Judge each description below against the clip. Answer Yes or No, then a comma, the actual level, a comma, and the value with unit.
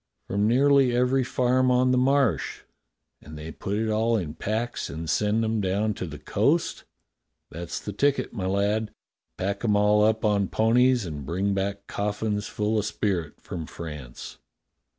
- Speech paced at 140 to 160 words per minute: No, average, 170 wpm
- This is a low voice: Yes, low, 105 Hz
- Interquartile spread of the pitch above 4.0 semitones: No, average, 3.6 semitones